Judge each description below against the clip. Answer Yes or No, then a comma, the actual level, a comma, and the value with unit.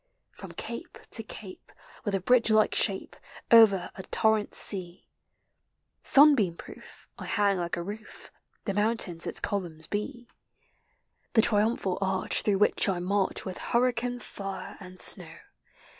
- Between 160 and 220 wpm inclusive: No, average, 140 wpm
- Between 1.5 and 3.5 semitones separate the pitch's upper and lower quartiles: Yes, average, 3.1 semitones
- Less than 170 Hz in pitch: No, high, 205 Hz